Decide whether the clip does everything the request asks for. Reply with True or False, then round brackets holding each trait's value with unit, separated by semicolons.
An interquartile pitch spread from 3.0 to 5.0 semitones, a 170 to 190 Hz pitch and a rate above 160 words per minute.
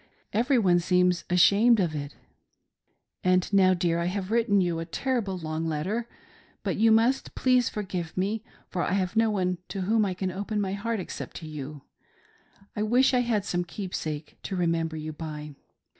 True (4.3 semitones; 185 Hz; 180 wpm)